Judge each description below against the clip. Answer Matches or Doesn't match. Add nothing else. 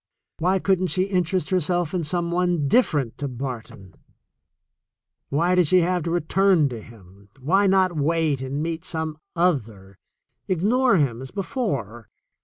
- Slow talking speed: Doesn't match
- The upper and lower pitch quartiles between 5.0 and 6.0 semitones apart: Matches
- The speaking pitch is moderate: Matches